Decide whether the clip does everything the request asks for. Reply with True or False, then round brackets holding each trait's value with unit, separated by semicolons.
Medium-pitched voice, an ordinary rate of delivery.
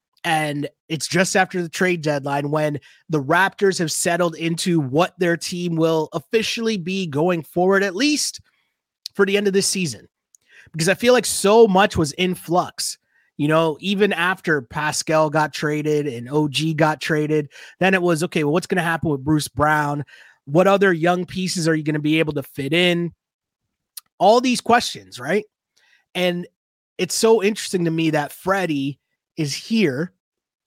True (170 Hz; 170 wpm)